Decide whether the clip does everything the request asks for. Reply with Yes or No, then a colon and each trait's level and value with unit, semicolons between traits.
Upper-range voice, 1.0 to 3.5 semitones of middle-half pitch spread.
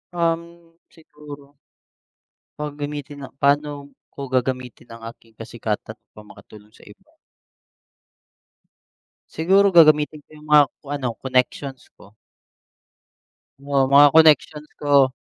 No: medium, 145 Hz; narrow, 2.6 semitones